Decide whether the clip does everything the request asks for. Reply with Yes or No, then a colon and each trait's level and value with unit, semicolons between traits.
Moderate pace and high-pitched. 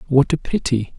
No: average, 185 wpm; medium, 140 Hz